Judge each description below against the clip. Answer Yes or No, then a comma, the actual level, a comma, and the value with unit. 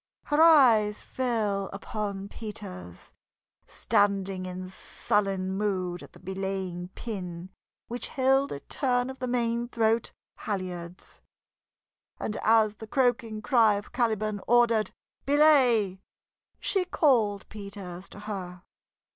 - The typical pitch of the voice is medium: No, high, 210 Hz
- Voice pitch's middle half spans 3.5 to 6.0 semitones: Yes, average, 3.9 semitones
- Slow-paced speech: Yes, slow, 115 wpm